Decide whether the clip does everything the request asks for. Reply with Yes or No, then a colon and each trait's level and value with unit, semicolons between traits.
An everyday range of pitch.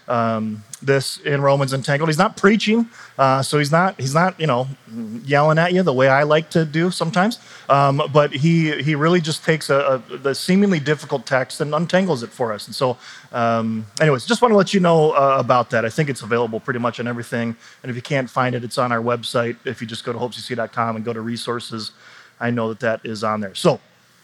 Yes: average, 5.0 semitones